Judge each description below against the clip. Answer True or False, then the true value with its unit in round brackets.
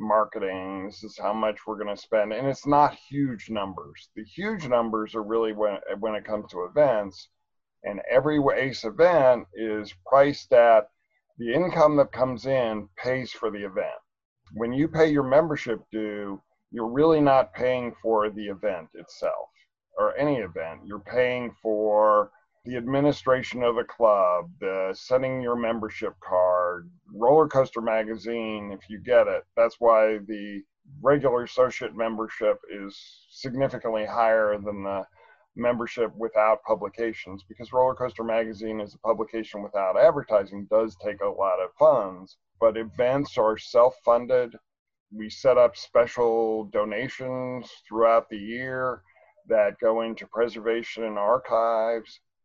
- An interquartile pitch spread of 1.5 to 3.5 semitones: True (3.1 semitones)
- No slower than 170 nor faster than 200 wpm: False (145 wpm)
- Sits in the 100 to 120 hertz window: True (115 Hz)